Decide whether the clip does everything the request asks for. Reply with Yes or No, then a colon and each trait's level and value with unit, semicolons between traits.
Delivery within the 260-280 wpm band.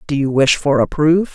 Yes: fast, 270 wpm